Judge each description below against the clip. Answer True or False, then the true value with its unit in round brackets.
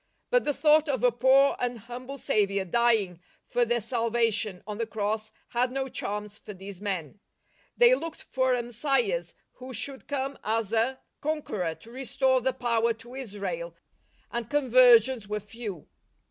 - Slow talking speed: False (160 wpm)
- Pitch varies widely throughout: False (3.8 semitones)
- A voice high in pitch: True (240 Hz)